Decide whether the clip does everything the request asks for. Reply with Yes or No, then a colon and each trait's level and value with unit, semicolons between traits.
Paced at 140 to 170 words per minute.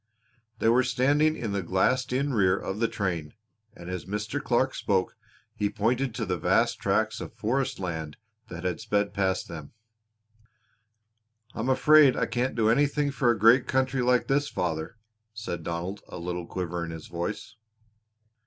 Yes: average, 160 wpm